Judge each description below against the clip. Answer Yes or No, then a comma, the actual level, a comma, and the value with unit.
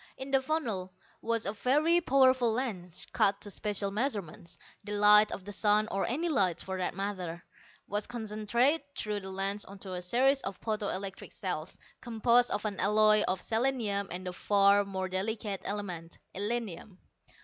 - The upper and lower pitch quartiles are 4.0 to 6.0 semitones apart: No, average, 3.4 semitones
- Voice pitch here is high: Yes, high, 205 Hz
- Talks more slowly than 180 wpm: Yes, average, 165 wpm